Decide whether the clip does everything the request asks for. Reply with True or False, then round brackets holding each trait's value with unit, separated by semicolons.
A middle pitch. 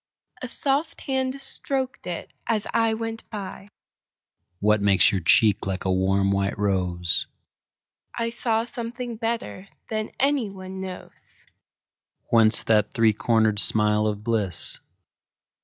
True (180 Hz)